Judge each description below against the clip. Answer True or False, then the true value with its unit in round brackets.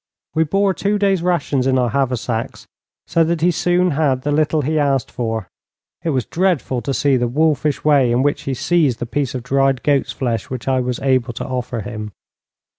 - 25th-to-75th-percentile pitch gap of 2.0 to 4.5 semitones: True (4.0 semitones)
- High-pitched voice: False (135 Hz)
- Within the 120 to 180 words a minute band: False (200 wpm)